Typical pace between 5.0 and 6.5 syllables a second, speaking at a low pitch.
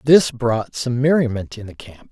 No: 4.6 syllables/s; low, 125 Hz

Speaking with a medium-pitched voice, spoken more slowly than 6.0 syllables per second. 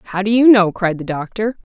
No: high, 200 Hz; 5.1 syllables/s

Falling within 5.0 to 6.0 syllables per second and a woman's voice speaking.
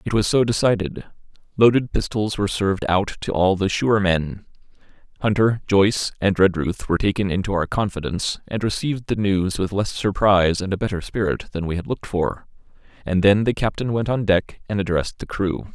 No: 5.6 syllables/s; male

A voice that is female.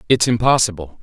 No: male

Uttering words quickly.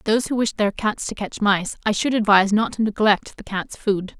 Yes: fast, 245 wpm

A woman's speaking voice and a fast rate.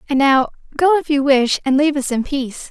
Yes: female; fast, 245 wpm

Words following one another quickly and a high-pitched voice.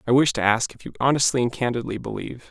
No: fast, 240 wpm; low, 125 Hz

